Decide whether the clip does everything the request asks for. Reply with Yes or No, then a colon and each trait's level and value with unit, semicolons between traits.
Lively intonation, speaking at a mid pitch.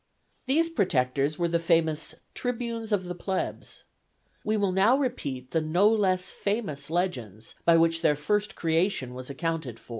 Yes: wide, 5.7 semitones; medium, 170 Hz